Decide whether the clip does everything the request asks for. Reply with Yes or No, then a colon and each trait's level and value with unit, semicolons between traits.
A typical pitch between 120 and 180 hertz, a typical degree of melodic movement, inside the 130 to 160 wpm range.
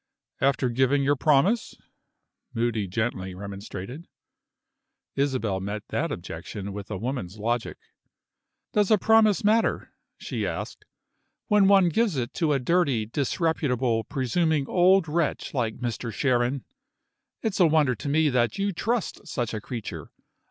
No: low, 135 Hz; wide, 6.9 semitones; slow, 135 wpm